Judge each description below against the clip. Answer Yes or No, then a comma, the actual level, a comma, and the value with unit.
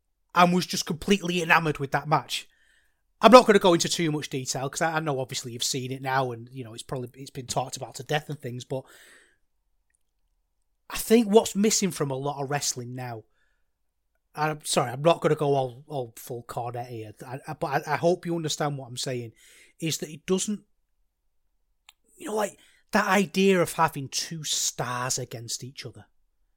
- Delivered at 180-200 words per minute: Yes, average, 195 wpm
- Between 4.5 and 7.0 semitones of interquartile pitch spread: Yes, average, 5.2 semitones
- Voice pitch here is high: No, low, 135 Hz